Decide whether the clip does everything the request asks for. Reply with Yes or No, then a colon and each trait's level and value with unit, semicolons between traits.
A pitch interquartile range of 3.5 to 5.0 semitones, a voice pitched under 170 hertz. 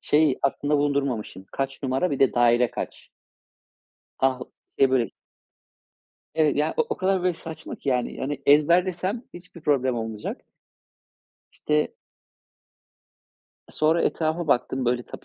Yes: average, 3.8 semitones; medium, 140 Hz